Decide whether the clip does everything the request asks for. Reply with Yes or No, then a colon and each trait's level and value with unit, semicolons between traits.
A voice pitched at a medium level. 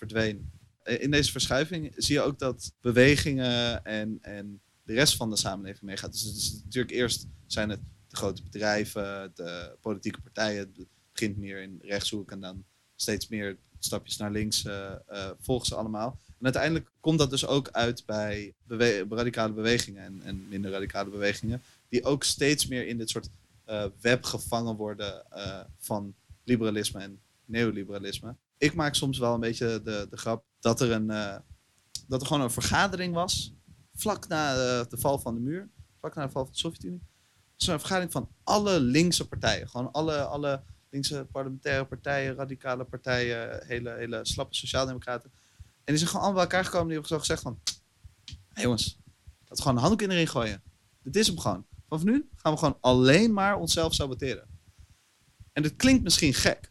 No: low, 115 Hz